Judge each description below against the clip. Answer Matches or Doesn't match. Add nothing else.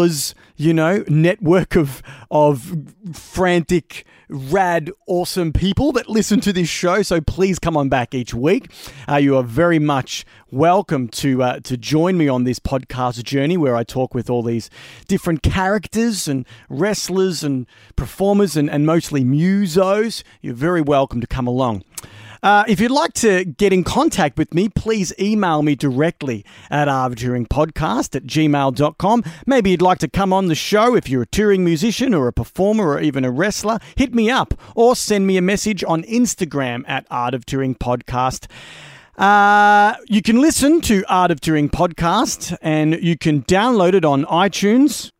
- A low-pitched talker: Doesn't match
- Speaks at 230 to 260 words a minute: Doesn't match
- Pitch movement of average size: Doesn't match